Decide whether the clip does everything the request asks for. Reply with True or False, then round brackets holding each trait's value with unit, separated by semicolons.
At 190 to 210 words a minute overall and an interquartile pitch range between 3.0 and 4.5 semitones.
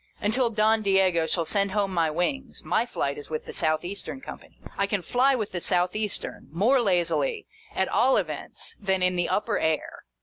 True (195 wpm; 4.0 semitones)